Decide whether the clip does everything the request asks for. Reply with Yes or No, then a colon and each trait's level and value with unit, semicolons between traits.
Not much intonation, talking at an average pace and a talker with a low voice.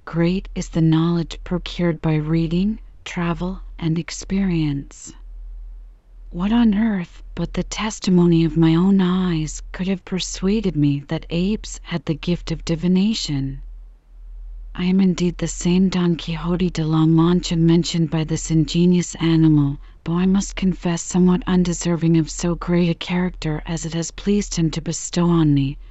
No: narrow, 2.0 semitones; average, 155 wpm; medium, 170 Hz